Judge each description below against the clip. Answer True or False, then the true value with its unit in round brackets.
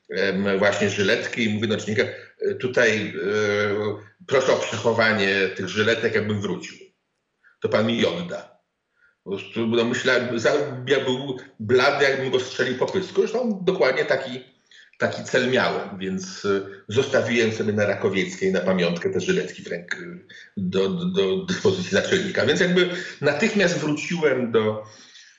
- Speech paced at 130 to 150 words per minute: True (140 wpm)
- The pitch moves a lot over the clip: True (6.5 semitones)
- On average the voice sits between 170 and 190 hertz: False (115 Hz)